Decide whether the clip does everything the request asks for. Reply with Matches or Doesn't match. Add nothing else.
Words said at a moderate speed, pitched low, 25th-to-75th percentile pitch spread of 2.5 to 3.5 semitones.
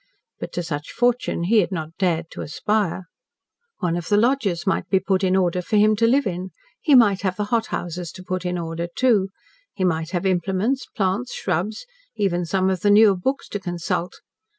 Doesn't match